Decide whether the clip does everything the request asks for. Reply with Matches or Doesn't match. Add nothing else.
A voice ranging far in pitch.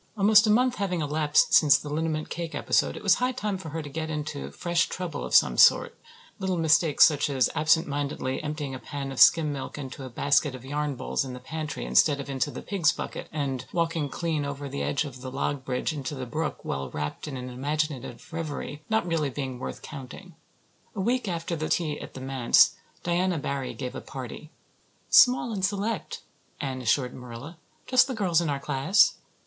Doesn't match